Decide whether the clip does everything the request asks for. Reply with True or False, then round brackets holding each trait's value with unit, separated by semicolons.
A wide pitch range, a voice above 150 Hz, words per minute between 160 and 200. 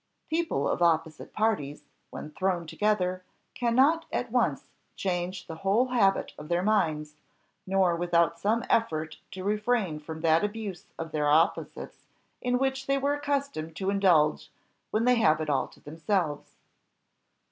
False (5.8 semitones; 185 Hz; 145 wpm)